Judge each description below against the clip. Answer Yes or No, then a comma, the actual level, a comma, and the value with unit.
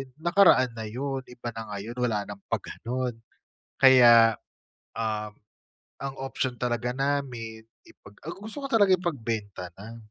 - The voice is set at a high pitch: No, low, 120 Hz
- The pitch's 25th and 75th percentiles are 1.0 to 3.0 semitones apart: No, average, 3.5 semitones